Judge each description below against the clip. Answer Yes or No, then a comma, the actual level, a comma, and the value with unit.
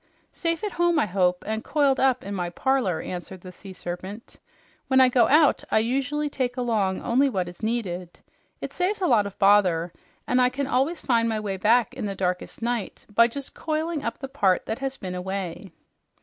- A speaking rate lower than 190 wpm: No, fast, 205 wpm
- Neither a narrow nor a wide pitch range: No, wide, 6.0 semitones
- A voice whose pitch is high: Yes, high, 230 Hz